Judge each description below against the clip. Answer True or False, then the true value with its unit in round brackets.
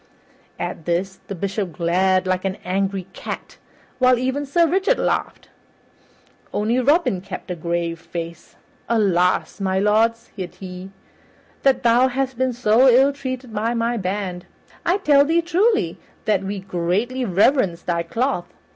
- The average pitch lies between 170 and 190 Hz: False (210 Hz)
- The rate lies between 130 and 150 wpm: True (145 wpm)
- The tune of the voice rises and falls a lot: True (6.0 semitones)